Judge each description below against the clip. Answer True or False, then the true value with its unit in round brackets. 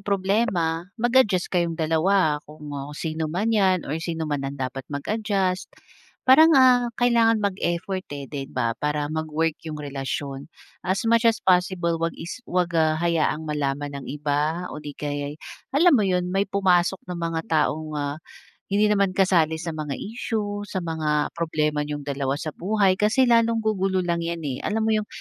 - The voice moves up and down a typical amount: True (4.8 semitones)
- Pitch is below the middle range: False (170 Hz)